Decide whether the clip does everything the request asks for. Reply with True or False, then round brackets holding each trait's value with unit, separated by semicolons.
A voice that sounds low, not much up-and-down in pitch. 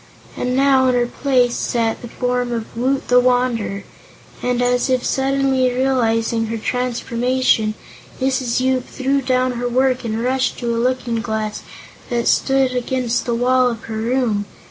False (250 Hz; 1.8 semitones)